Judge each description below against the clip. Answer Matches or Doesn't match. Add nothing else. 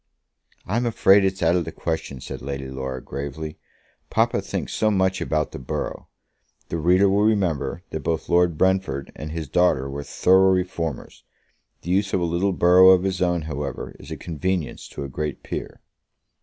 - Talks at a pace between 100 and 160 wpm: Doesn't match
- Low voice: Matches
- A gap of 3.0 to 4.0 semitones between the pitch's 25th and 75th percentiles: Doesn't match